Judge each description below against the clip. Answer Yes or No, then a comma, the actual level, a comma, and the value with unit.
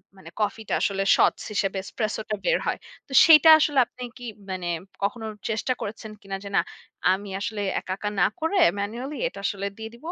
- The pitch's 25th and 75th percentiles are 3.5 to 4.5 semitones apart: Yes, average, 4.0 semitones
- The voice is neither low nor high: No, high, 215 Hz